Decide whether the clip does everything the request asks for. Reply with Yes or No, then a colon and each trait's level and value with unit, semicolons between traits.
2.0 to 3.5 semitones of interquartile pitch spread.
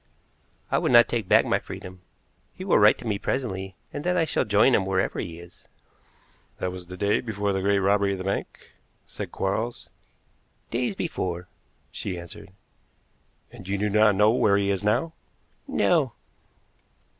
Yes: average, 2.8 semitones